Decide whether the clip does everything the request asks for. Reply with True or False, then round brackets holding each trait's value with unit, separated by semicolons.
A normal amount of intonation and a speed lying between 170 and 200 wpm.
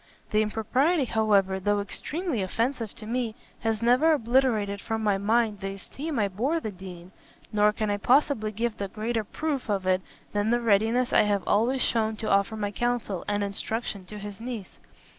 True (3.0 semitones; 180 wpm)